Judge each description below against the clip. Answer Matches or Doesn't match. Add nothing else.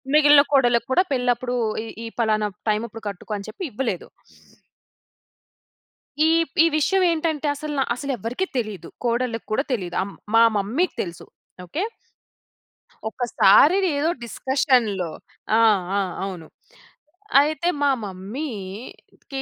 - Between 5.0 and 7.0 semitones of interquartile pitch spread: Matches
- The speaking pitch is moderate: Doesn't match